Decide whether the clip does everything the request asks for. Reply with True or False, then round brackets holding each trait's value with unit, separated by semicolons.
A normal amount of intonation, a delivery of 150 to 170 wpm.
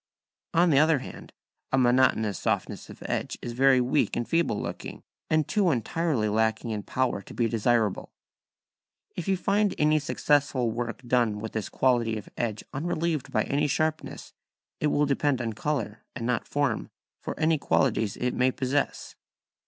True (4.7 semitones; 165 wpm)